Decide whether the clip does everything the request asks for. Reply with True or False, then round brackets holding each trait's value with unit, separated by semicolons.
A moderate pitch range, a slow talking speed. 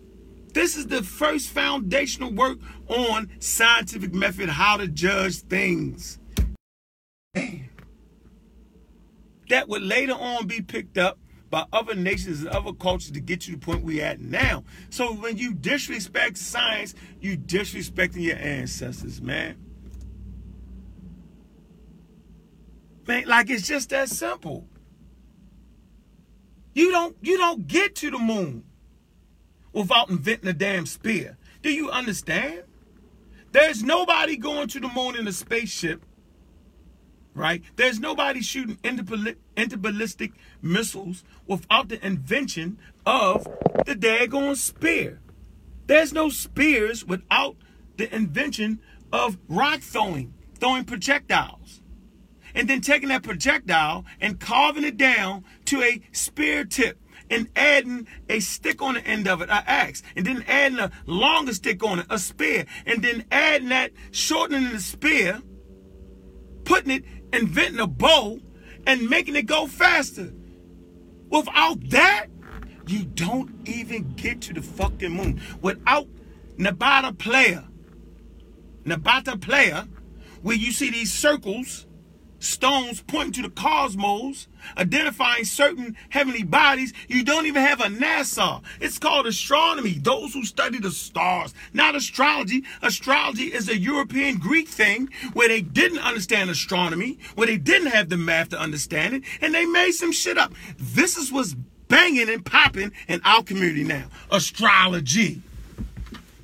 False (6.6 semitones; 130 wpm)